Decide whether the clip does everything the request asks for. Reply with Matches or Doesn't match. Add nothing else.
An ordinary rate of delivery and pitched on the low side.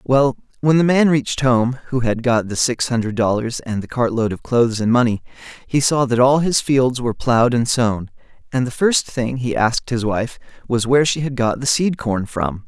Doesn't match